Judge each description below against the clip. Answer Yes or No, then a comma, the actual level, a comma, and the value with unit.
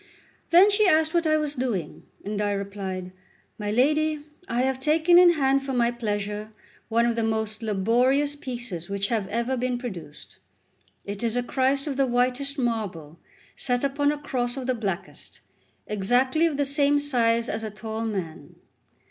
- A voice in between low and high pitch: No, high, 245 Hz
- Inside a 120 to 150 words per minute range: No, average, 175 wpm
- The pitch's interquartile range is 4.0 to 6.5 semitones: Yes, average, 5.0 semitones